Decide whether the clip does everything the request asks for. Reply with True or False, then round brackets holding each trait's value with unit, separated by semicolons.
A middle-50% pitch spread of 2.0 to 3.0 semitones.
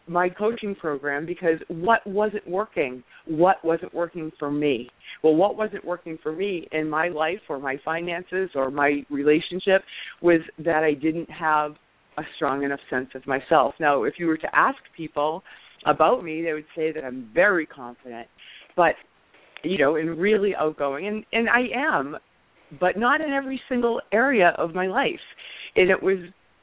False (4.0 semitones)